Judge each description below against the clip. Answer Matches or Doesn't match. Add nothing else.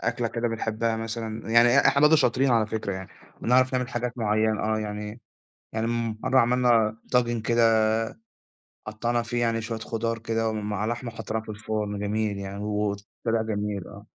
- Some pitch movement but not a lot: Doesn't match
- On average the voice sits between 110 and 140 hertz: Matches